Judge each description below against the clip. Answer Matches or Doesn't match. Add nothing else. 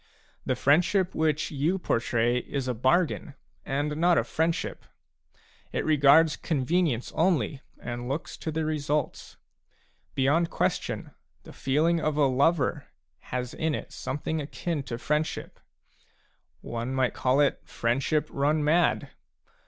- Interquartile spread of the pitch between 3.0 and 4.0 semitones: Matches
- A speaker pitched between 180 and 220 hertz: Doesn't match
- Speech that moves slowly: Matches